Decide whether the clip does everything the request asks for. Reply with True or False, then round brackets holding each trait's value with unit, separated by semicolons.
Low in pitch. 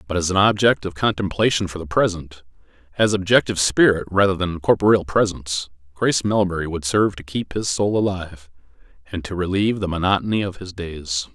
True (90 Hz)